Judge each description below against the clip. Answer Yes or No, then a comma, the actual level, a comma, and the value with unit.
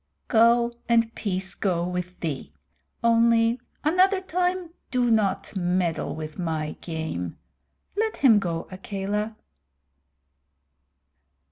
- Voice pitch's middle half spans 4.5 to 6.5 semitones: Yes, average, 5.1 semitones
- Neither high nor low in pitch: No, high, 210 Hz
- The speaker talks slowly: Yes, slow, 100 wpm